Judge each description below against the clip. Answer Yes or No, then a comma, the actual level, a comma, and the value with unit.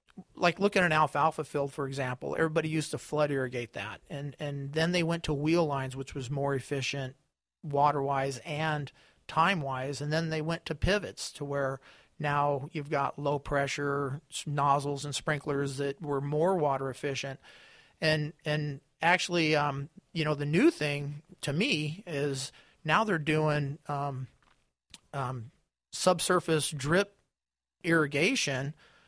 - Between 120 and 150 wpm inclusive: Yes, average, 140 wpm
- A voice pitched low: No, medium, 145 Hz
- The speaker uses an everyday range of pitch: No, narrow, 2.2 semitones